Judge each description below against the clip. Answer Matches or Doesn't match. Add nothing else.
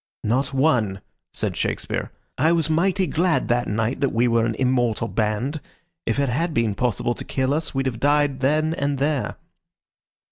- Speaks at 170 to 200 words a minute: Matches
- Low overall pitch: Matches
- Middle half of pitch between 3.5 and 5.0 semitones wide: Matches